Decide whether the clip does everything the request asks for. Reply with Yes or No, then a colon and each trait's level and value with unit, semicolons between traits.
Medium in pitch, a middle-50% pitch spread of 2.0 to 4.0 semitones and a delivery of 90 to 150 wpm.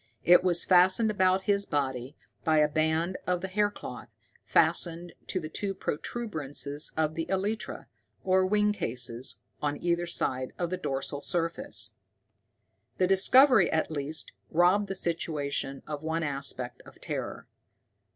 No: medium, 170 Hz; average, 4.4 semitones; average, 140 wpm